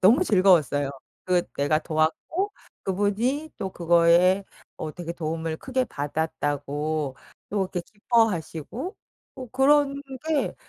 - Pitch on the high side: No, medium, 180 Hz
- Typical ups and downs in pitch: No, wide, 7.6 semitones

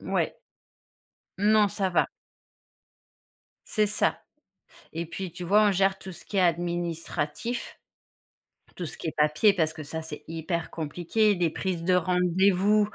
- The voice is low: No, medium, 180 Hz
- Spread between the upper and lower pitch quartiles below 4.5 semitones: Yes, average, 3.2 semitones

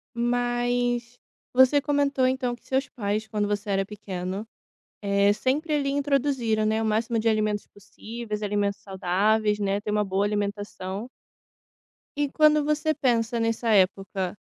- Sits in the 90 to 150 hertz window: No, high, 220 Hz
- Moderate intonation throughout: Yes, average, 3.5 semitones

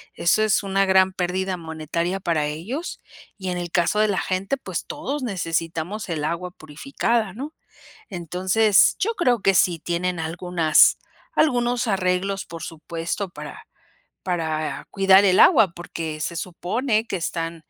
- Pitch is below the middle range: No, medium, 185 Hz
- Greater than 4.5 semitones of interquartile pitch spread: No, average, 3.8 semitones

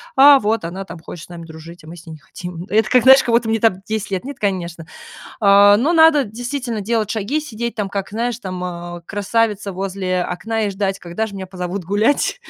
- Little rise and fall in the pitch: No, average, 4.1 semitones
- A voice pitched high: Yes, high, 205 Hz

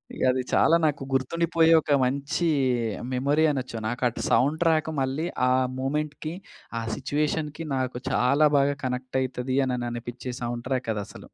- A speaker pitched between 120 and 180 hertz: Yes, low, 135 Hz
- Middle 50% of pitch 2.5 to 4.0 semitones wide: Yes, average, 3.2 semitones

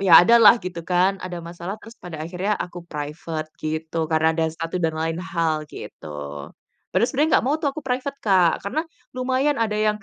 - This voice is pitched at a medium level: Yes, medium, 175 Hz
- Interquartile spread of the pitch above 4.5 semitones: Yes, wide, 5.5 semitones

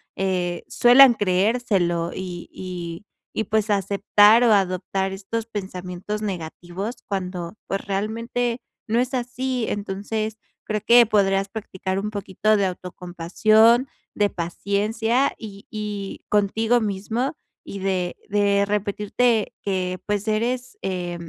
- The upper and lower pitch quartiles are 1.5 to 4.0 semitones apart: Yes, average, 2.9 semitones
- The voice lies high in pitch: Yes, high, 205 Hz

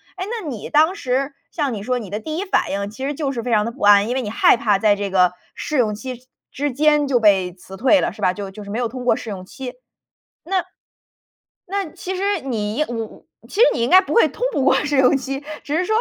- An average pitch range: No, wide, 6.1 semitones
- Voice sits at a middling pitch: No, very high, 255 Hz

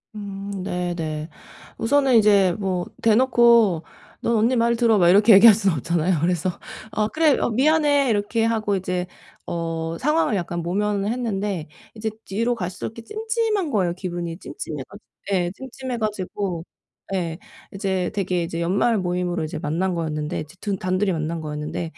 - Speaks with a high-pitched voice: Yes, high, 195 Hz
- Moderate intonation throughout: Yes, average, 4.6 semitones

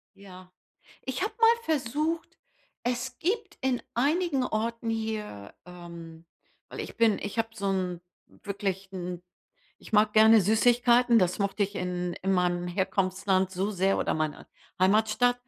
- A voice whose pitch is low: No, high, 210 Hz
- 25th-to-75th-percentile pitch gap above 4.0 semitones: Yes, average, 4.8 semitones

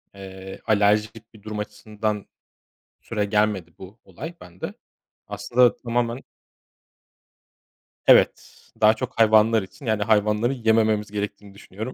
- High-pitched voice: No, low, 105 Hz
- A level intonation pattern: Yes, narrow, 1.7 semitones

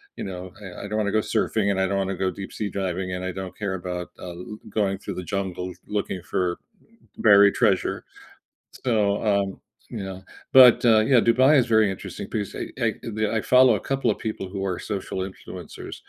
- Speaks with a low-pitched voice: Yes, low, 100 Hz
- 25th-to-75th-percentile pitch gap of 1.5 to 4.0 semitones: Yes, narrow, 2.5 semitones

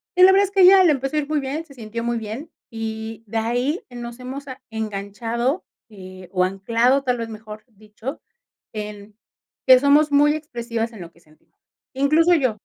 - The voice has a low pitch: No, high, 235 Hz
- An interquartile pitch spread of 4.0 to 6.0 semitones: Yes, average, 4.7 semitones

